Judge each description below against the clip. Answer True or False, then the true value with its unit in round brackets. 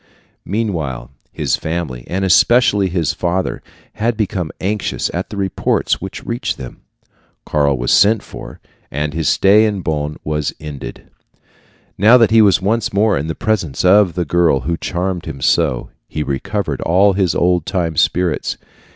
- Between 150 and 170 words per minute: True (160 wpm)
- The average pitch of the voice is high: False (90 Hz)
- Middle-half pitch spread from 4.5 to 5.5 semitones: True (5.0 semitones)